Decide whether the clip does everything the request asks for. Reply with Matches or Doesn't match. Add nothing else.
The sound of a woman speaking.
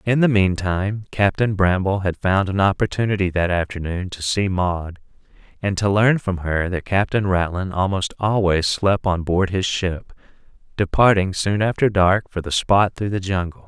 Doesn't match